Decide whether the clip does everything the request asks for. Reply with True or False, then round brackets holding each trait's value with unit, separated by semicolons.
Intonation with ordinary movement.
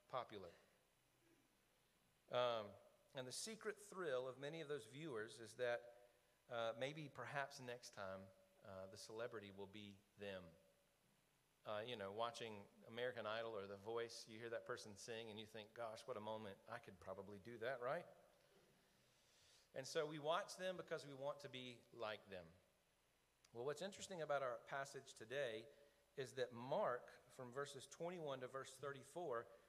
True (4.7 semitones)